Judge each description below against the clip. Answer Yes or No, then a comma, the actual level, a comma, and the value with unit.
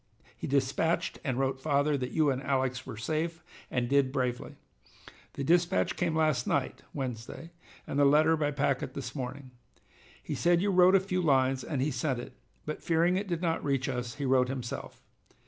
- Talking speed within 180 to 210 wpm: Yes, average, 185 wpm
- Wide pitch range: No, average, 3.8 semitones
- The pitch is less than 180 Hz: Yes, medium, 140 Hz